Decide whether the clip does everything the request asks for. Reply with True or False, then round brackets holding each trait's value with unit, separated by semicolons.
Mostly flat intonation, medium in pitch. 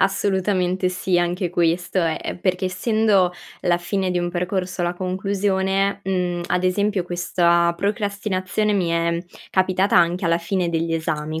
True (1.8 semitones; 180 Hz)